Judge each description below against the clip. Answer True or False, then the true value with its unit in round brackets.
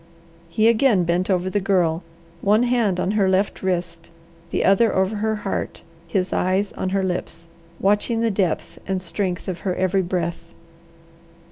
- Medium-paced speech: True (160 wpm)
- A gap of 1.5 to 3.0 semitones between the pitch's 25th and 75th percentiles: True (2.4 semitones)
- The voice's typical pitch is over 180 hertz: True (190 Hz)